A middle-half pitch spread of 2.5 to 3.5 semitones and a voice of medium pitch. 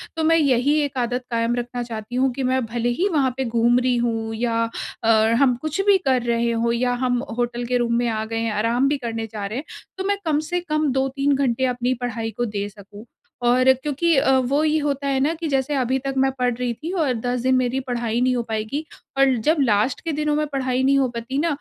No: average, 2.9 semitones; very high, 250 Hz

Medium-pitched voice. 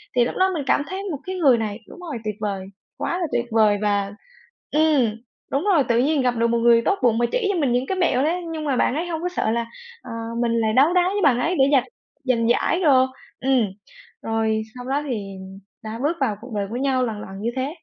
No: very high, 255 Hz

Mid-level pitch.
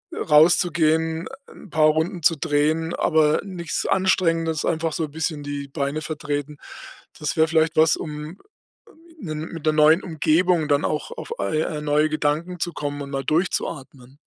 Yes: medium, 155 Hz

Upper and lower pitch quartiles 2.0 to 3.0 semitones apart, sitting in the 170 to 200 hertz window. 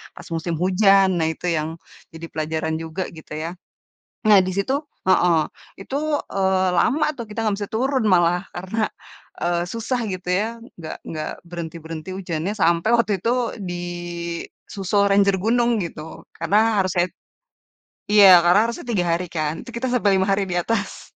No: average, 4.0 semitones; medium, 185 Hz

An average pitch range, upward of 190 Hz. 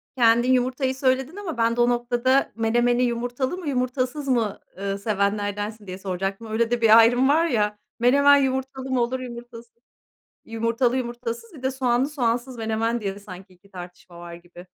Yes: average, 3.3 semitones; high, 240 Hz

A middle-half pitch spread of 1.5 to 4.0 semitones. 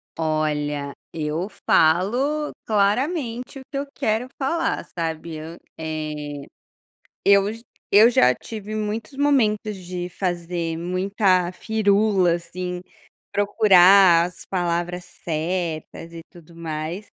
No: average, 4.5 semitones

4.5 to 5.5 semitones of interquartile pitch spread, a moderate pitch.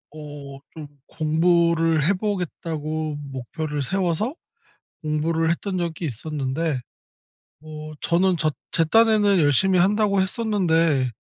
No: average, 3.5 semitones; medium, 165 Hz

